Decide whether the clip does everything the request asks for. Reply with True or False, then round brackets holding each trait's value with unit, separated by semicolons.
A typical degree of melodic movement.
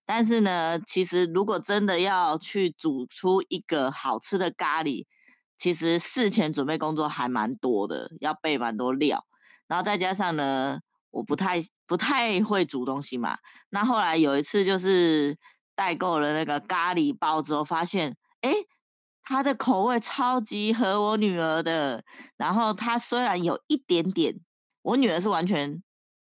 False (5.7 semitones)